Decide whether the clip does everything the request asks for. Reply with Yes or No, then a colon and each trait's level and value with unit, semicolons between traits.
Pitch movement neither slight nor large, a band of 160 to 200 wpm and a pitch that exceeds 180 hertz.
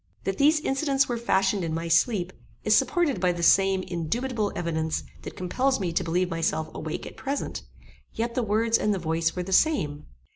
No: wide, 6.2 semitones; average, 190 wpm; high, 190 Hz